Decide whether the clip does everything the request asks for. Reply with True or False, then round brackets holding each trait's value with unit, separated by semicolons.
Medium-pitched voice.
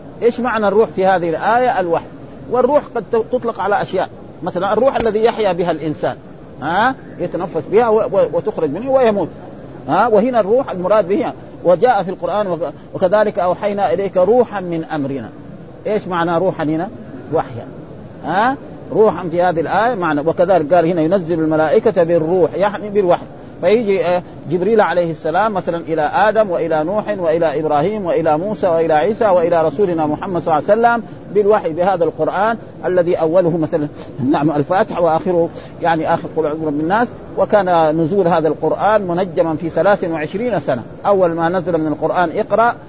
True (175 Hz)